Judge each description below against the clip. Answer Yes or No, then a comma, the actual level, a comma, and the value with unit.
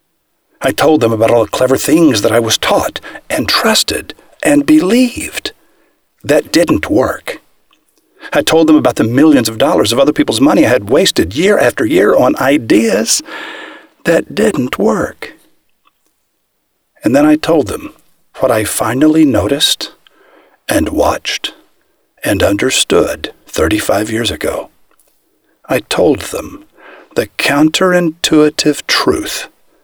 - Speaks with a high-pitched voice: Yes, very high, 290 Hz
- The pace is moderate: No, slow, 130 wpm